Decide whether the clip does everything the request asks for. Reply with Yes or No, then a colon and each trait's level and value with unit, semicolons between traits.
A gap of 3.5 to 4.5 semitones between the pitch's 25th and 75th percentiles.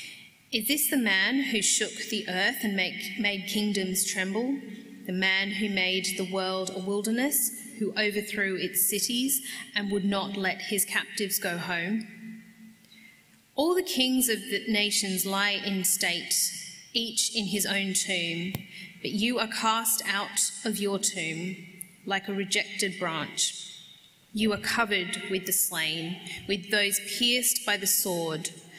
No: average, 2.9 semitones